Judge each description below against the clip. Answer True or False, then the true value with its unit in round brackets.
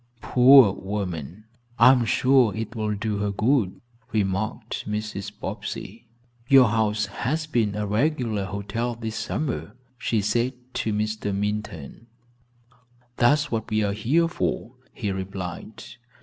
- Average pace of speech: False (130 wpm)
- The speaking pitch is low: True (110 Hz)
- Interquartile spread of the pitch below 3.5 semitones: True (3.0 semitones)